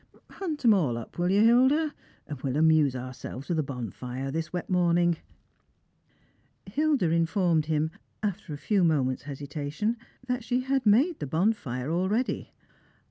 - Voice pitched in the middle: Yes, medium, 170 Hz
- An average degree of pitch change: No, wide, 7.4 semitones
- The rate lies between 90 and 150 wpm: Yes, average, 145 wpm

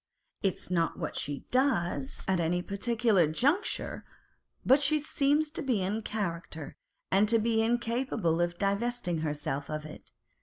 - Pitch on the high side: Yes, high, 200 Hz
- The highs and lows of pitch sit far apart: Yes, wide, 6.4 semitones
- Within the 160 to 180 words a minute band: No, average, 150 wpm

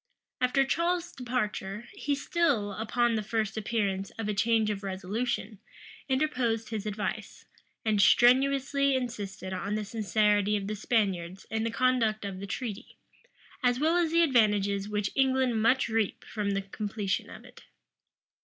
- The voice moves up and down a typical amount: Yes, average, 3.7 semitones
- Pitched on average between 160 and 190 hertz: No, high, 220 Hz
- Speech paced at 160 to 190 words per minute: No, average, 150 wpm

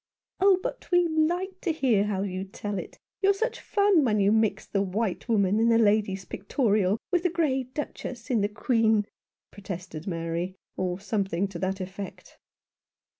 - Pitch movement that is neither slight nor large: No, wide, 6.0 semitones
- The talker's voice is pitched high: Yes, high, 210 Hz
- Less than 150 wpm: No, average, 170 wpm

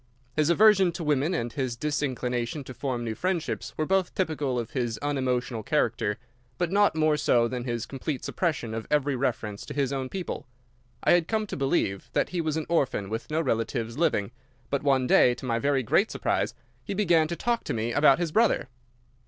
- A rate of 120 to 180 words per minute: No, average, 200 wpm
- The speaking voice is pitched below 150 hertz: Yes, medium, 140 Hz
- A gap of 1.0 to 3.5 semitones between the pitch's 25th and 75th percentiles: No, average, 5.3 semitones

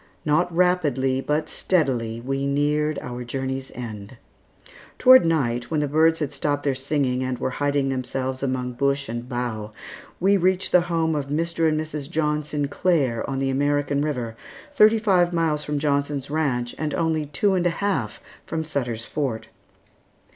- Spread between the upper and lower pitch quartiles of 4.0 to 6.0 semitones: No, average, 3.5 semitones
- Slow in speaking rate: No, average, 160 wpm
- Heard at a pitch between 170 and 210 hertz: No, medium, 145 Hz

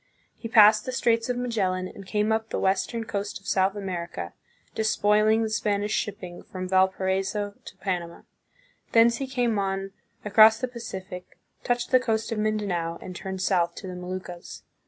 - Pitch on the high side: Yes, high, 205 Hz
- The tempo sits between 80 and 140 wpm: No, average, 165 wpm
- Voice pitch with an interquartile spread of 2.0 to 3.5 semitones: Yes, average, 2.9 semitones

